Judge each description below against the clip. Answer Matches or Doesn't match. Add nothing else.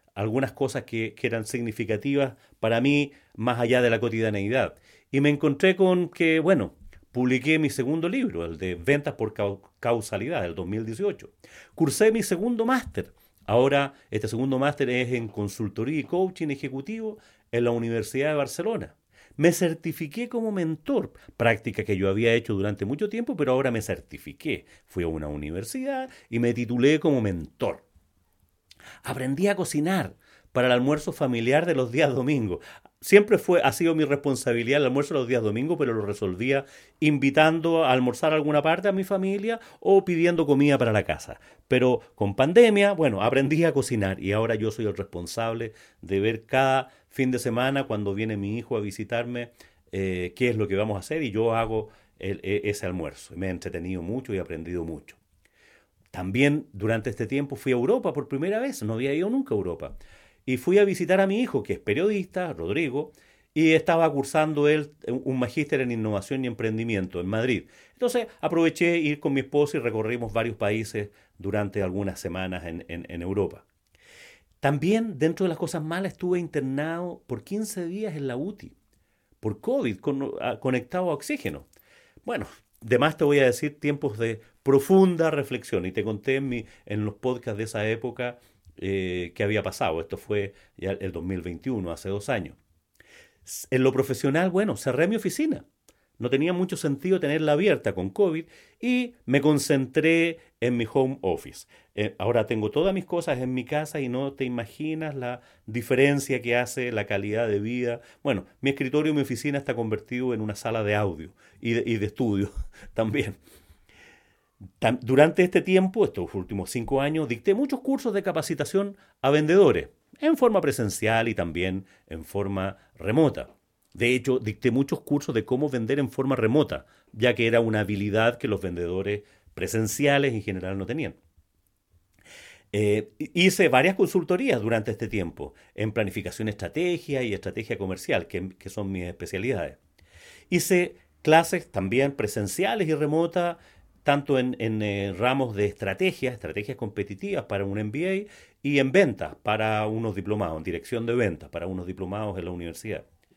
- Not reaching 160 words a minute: Doesn't match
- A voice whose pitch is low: Matches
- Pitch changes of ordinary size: Doesn't match